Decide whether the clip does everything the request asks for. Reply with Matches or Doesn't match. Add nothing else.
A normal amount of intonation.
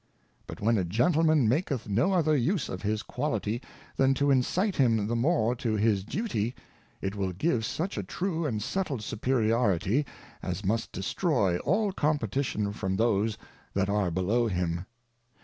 Doesn't match